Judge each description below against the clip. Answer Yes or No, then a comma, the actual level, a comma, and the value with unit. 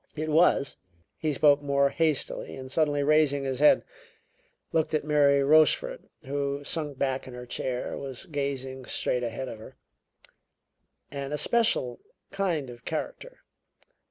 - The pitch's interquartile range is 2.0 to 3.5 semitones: Yes, average, 2.7 semitones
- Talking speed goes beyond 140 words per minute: No, slow, 135 wpm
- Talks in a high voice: No, medium, 140 Hz